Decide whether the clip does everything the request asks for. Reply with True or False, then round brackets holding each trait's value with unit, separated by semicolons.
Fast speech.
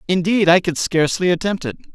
False (185 wpm)